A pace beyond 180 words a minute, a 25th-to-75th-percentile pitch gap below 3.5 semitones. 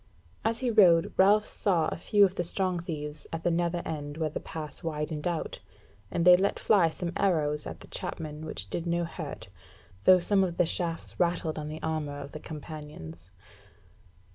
Yes: average, 190 wpm; average, 2.8 semitones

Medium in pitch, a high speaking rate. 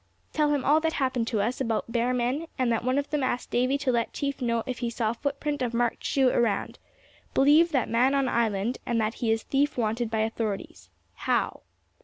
No: high, 245 Hz; fast, 215 wpm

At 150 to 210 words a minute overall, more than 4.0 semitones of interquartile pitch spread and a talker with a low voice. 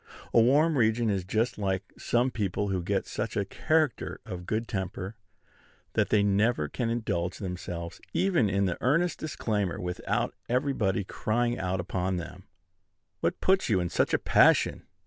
Yes: average, 160 wpm; average, 4.6 semitones; low, 105 Hz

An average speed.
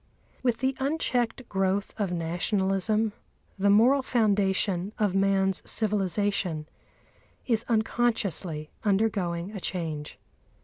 No: slow, 95 wpm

